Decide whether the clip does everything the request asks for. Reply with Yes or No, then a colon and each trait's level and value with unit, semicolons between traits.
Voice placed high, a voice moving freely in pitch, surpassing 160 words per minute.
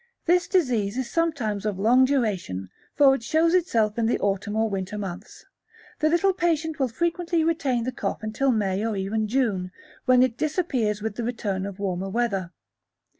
Yes: high, 230 Hz; wide, 6.3 semitones; average, 180 wpm